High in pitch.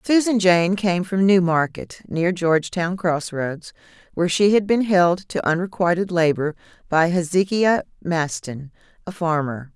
No: medium, 175 Hz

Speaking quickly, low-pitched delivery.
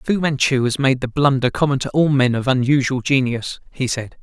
Yes: fast, 215 wpm; low, 130 Hz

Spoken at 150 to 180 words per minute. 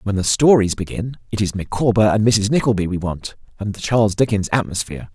No: average, 200 wpm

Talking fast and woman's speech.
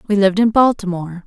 No: average, 190 wpm; female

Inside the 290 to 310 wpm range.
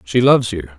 No: fast, 230 wpm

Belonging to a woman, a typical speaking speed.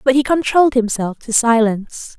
Yes: female; average, 165 wpm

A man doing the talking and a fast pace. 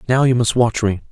Yes: male; fast, 270 wpm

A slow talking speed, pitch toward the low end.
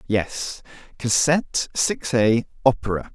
Yes: slow, 75 wpm; low, 120 Hz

